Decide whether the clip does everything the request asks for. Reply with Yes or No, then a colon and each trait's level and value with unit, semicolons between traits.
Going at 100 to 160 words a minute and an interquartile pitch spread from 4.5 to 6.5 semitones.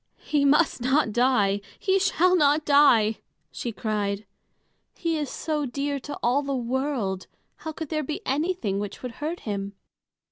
Yes: average, 155 wpm; wide, 5.5 semitones